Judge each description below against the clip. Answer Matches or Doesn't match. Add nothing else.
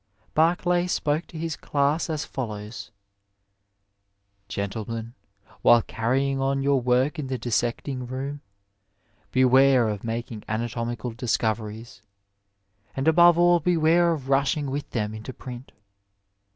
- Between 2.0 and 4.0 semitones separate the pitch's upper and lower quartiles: Doesn't match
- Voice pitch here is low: Matches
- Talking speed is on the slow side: Matches